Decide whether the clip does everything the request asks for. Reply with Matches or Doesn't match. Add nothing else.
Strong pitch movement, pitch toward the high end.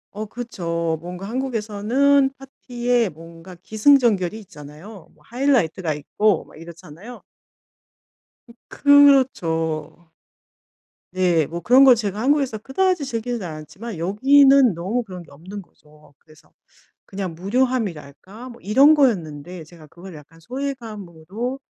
Matches